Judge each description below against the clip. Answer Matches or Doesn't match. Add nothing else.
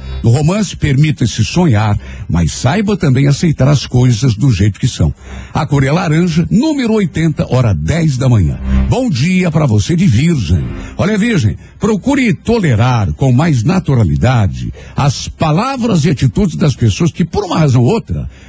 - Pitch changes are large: Matches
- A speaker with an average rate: Matches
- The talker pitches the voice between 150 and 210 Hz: Doesn't match